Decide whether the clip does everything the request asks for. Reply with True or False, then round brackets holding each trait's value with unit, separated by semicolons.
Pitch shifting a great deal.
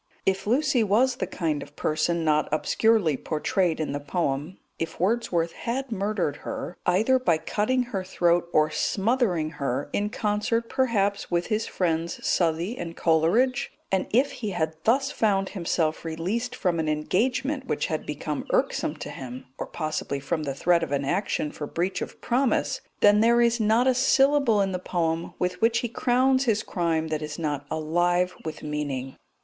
True (6.4 semitones)